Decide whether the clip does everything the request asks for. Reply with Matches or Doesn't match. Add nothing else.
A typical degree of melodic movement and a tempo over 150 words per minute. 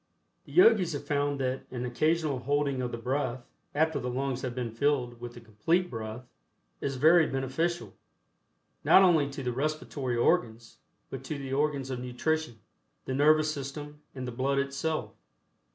Matches